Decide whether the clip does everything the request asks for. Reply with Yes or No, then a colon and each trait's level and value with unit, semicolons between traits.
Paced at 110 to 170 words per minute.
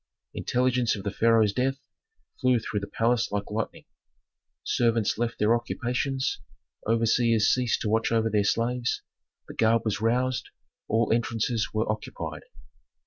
Yes: average, 140 wpm